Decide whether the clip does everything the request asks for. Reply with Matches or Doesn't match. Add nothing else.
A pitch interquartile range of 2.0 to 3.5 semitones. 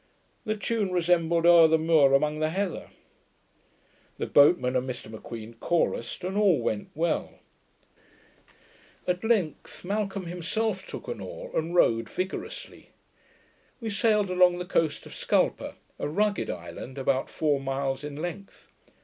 Doesn't match